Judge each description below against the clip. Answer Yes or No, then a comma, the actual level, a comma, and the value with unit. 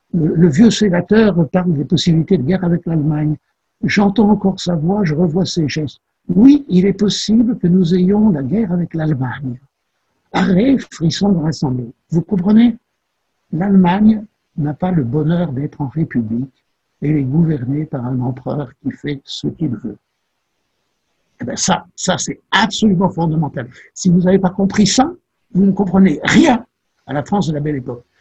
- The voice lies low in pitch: No, medium, 175 Hz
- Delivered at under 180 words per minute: Yes, average, 170 wpm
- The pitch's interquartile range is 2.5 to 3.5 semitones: No, average, 4.9 semitones